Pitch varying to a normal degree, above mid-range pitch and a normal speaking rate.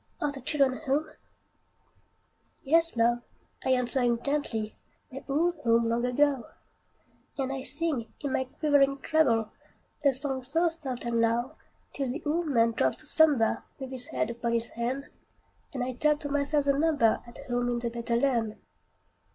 Yes: average, 3.4 semitones; very high, 260 Hz; average, 165 wpm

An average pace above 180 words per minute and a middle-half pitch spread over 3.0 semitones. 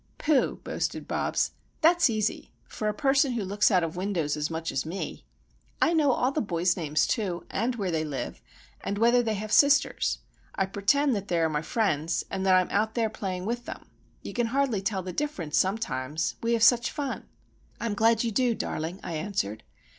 Yes: average, 195 wpm; average, 5.3 semitones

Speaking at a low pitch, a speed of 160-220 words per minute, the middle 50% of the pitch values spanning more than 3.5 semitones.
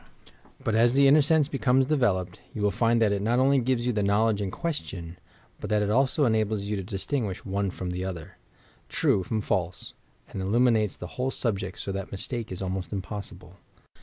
Yes: low, 105 Hz; average, 200 wpm; average, 4.4 semitones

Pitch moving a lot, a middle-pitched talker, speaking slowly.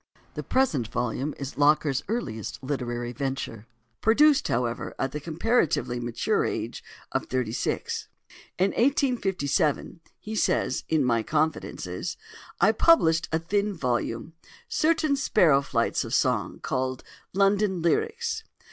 Yes: wide, 8.8 semitones; medium, 155 Hz; slow, 120 wpm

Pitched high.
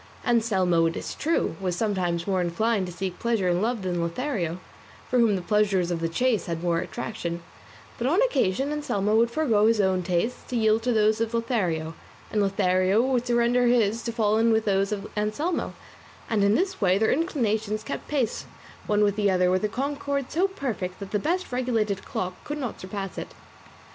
Yes: high, 215 Hz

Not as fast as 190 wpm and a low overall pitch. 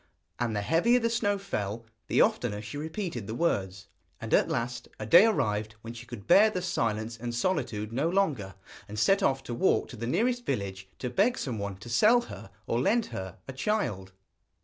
No: average, 195 wpm; low, 120 Hz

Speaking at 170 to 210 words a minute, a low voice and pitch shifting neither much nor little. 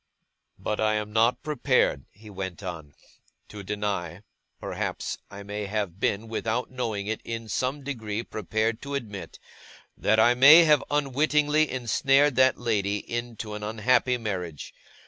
No: average, 145 wpm; low, 110 Hz; average, 3.8 semitones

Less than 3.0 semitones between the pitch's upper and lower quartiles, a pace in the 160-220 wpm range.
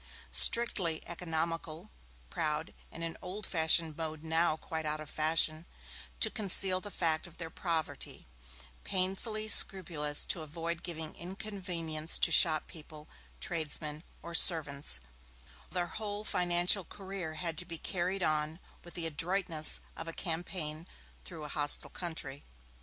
No: narrow, 2.6 semitones; slow, 135 wpm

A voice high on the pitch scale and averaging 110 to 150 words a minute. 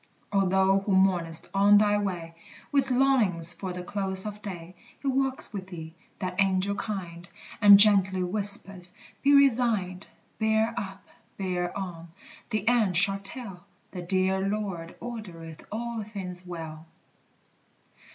Yes: high, 195 Hz; slow, 135 wpm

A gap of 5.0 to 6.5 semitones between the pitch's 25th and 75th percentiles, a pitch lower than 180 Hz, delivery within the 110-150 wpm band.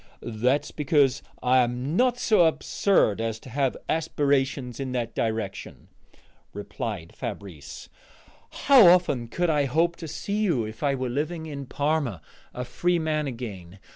Yes: average, 5.3 semitones; low, 135 Hz; average, 145 wpm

